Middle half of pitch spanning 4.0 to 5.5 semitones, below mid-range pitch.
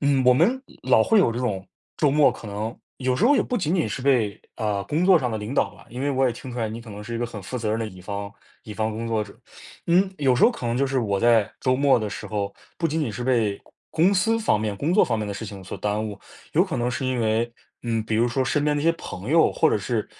Yes: average, 4.6 semitones; low, 120 Hz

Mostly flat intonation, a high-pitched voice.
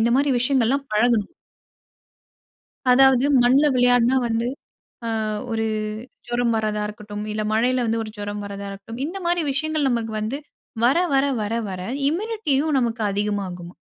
No: average, 4.2 semitones; high, 235 Hz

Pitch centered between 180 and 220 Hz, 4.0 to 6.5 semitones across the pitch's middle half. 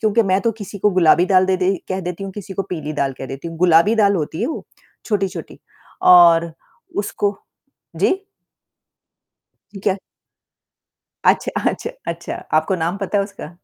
No: medium, 185 Hz; average, 3.2 semitones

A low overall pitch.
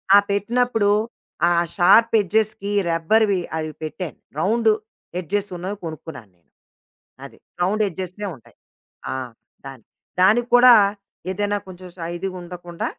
No: high, 190 Hz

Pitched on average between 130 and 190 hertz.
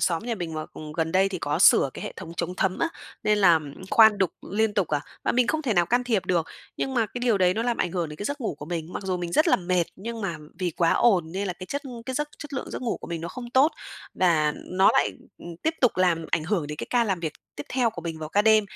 Yes: medium, 185 Hz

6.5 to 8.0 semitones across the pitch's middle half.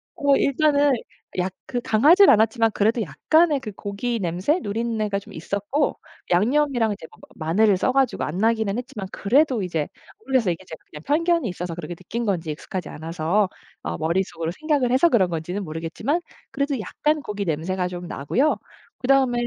Yes: wide, 7.2 semitones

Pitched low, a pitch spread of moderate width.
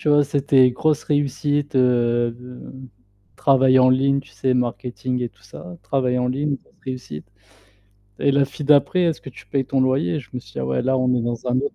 No: low, 130 Hz; narrow, 2.2 semitones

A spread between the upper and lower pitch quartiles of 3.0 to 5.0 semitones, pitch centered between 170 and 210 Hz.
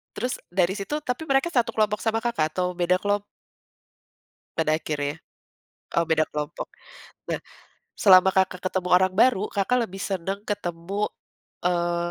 Yes: average, 3.4 semitones; high, 190 Hz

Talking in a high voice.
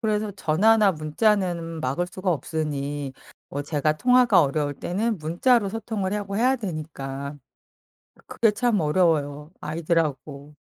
No: medium, 165 Hz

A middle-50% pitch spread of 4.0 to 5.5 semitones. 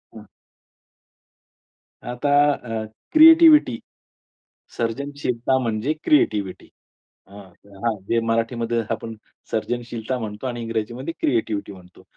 No: average, 2.8 semitones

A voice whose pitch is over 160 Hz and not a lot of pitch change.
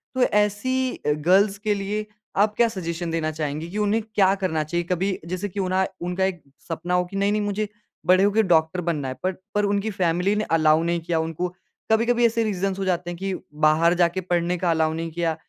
No: medium, 185 Hz; average, 3.4 semitones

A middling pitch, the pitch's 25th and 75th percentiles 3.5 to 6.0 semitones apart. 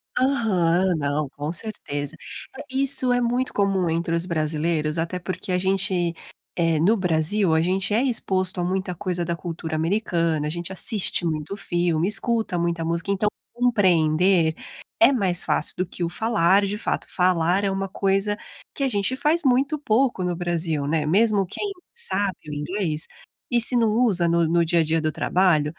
Yes: medium, 180 Hz; average, 4.0 semitones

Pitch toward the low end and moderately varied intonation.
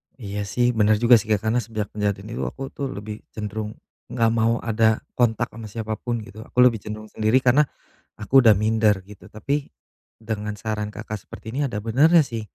No: low, 110 Hz; narrow, 2.1 semitones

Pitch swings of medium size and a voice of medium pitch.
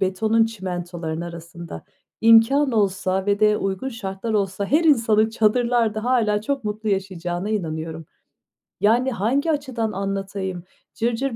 No: average, 3.4 semitones; high, 210 Hz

